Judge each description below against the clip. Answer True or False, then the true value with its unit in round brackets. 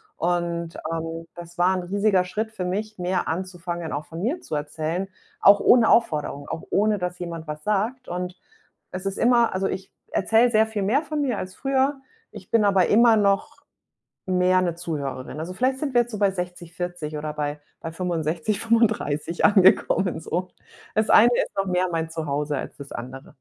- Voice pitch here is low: False (180 Hz)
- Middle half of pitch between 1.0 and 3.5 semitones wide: False (4.4 semitones)